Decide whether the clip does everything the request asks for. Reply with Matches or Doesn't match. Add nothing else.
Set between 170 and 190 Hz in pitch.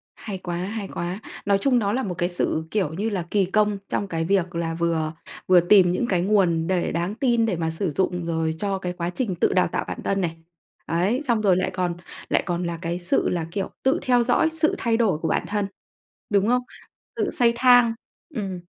Matches